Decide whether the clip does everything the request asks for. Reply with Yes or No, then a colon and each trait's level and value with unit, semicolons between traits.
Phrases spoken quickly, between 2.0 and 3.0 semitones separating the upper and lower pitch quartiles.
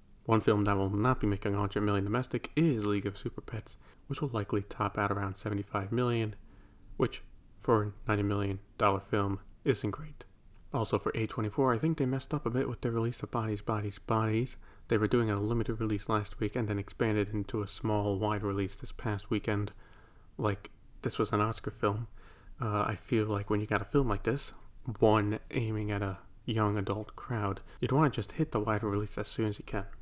Yes: fast, 210 wpm; narrow, 2.4 semitones